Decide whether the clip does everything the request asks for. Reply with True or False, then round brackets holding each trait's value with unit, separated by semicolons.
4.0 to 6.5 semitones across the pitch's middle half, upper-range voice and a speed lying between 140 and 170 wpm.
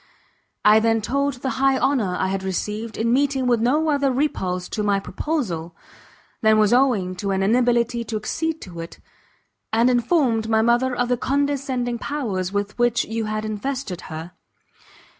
True (4.3 semitones; 230 Hz; 165 wpm)